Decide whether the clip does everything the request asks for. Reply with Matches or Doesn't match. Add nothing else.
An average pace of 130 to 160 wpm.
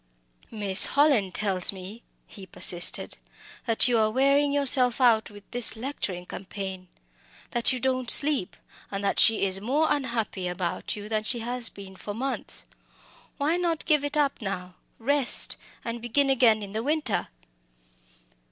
Matches